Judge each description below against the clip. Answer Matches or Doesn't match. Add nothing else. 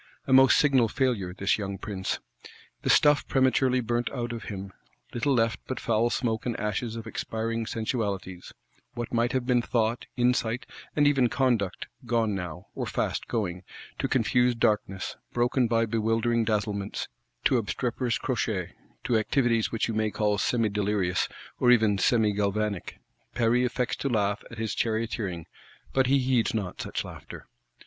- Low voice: Matches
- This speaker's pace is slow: Doesn't match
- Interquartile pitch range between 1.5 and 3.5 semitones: Matches